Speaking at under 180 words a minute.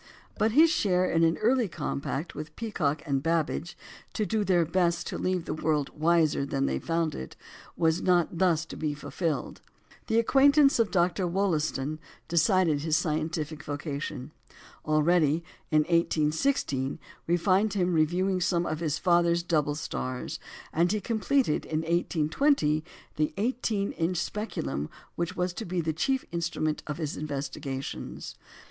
Yes: average, 150 wpm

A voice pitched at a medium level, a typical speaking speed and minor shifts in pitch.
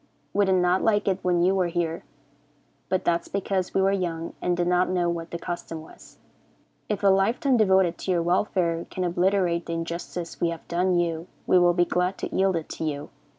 No: medium, 180 Hz; fast, 220 wpm; narrow, 1.9 semitones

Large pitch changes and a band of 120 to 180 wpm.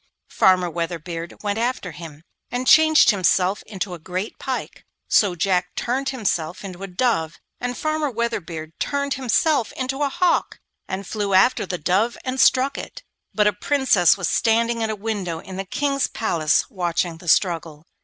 Yes: wide, 6.1 semitones; average, 165 wpm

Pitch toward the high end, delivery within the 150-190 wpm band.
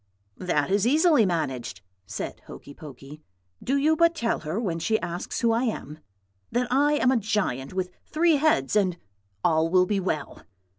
Yes: high, 195 Hz; average, 170 wpm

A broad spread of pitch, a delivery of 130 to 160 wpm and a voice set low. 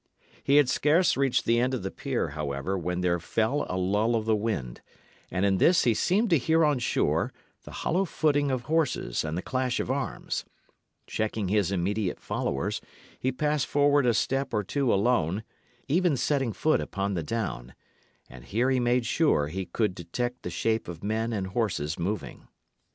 No: wide, 6.6 semitones; average, 185 wpm; low, 115 Hz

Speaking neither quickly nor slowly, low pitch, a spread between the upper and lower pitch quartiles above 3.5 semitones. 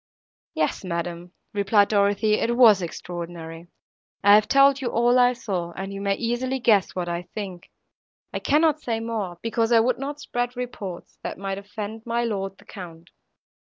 No: average, 170 wpm; high, 210 Hz; average, 4.5 semitones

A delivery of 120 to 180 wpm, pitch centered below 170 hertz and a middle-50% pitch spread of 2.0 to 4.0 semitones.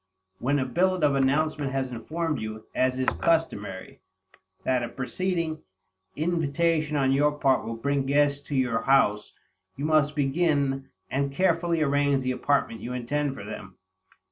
Yes: average, 150 wpm; medium, 140 Hz; average, 3.1 semitones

